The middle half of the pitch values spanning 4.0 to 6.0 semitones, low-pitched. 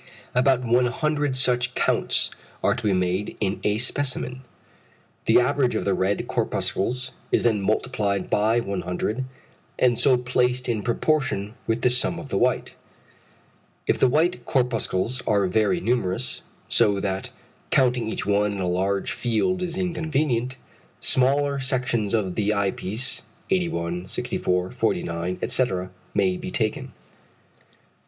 Yes: average, 4.5 semitones; low, 120 Hz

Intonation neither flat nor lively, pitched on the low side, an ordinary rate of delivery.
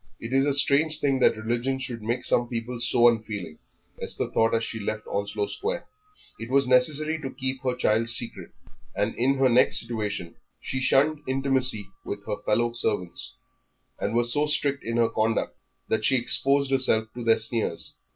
Yes: average, 3.2 semitones; low, 120 Hz; average, 180 wpm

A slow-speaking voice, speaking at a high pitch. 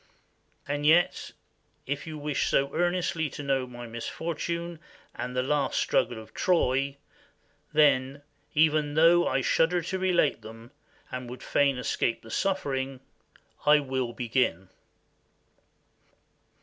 No: slow, 125 wpm; medium, 140 Hz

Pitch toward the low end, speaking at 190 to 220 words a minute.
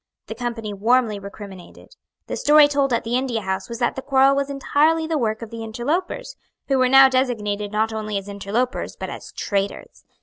No: high, 240 Hz; average, 195 wpm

